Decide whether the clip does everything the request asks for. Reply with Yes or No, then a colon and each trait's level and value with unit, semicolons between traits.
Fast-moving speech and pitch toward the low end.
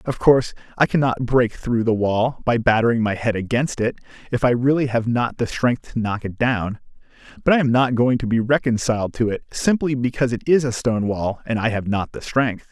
Yes: fast, 225 wpm; low, 120 Hz